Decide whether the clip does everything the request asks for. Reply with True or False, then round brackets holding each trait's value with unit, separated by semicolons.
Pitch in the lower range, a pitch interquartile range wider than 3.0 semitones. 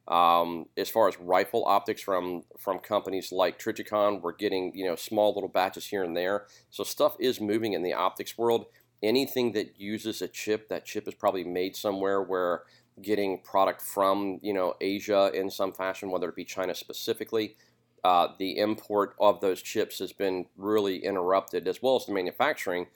False (100 Hz; 2.4 semitones)